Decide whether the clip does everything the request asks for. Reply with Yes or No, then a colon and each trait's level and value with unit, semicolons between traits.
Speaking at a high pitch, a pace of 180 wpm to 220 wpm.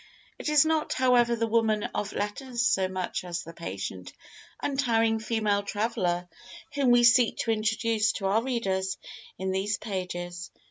No: high, 215 Hz; average, 150 wpm